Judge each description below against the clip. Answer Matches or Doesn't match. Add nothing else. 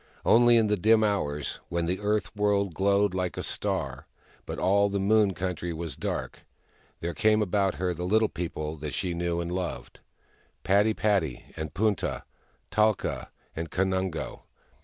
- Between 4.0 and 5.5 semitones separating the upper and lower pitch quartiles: Doesn't match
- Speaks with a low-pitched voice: Matches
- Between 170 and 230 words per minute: Doesn't match